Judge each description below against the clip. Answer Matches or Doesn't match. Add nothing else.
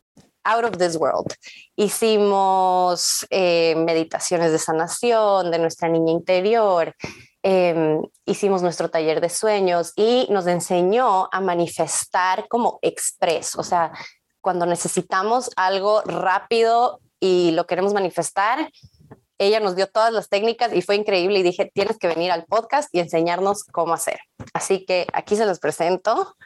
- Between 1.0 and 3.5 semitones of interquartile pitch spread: Matches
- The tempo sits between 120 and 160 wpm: Matches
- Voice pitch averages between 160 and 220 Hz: Matches